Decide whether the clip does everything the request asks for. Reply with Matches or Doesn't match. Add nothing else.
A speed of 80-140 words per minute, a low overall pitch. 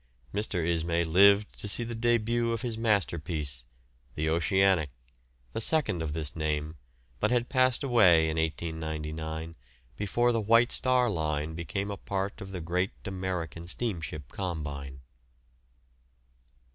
Matches